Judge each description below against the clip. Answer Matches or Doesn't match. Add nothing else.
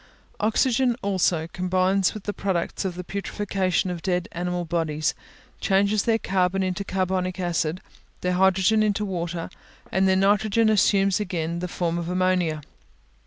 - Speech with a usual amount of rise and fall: Doesn't match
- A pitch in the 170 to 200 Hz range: Matches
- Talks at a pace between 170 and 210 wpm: Doesn't match